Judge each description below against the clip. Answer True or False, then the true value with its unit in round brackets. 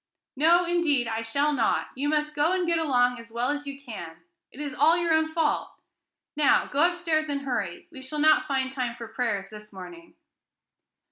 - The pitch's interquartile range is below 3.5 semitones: False (4.5 semitones)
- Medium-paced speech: True (195 wpm)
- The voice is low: False (285 Hz)